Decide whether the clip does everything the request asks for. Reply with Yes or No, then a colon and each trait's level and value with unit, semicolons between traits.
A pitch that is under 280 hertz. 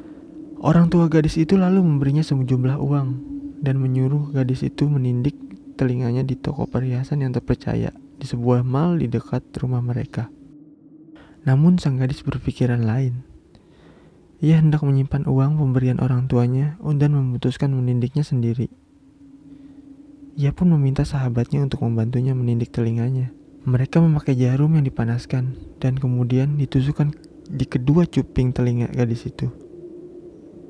Yes: medium, 140 Hz